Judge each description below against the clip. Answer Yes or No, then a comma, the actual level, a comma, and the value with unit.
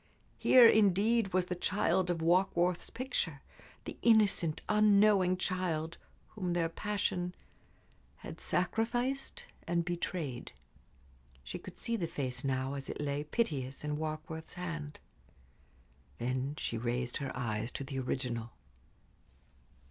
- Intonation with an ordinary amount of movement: No, wide, 5.8 semitones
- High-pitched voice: No, medium, 170 Hz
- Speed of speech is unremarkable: No, slow, 120 wpm